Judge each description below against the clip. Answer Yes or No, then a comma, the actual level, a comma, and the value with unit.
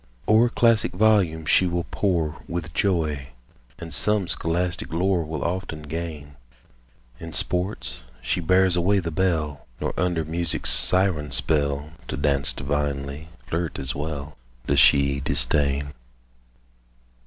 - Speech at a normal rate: No, slow, 125 wpm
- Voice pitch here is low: Yes, very low, 80 Hz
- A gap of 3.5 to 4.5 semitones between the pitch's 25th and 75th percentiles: Yes, average, 3.8 semitones